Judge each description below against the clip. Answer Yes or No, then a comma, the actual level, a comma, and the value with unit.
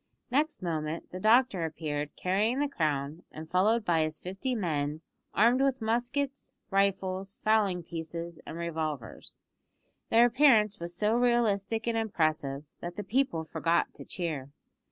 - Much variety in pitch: Yes, wide, 6.1 semitones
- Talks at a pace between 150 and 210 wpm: No, average, 140 wpm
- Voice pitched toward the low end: No, medium, 185 Hz